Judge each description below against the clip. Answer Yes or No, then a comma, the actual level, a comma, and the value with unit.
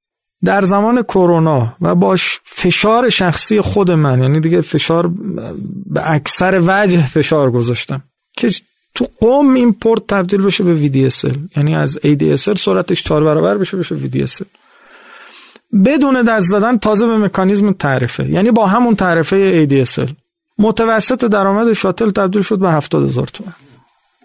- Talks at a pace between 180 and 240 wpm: No, average, 140 wpm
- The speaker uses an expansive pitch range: Yes, wide, 5.8 semitones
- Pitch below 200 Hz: Yes, high, 190 Hz